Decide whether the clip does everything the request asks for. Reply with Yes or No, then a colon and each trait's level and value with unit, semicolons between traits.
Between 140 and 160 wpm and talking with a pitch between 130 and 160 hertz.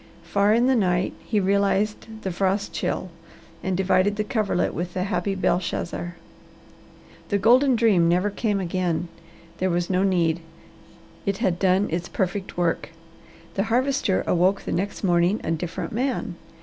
No: average, 150 wpm; high, 190 Hz